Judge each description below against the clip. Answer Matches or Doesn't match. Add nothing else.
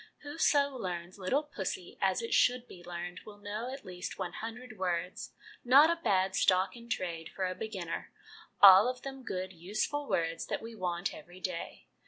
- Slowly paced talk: Doesn't match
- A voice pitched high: Matches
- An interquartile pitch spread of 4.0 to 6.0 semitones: Matches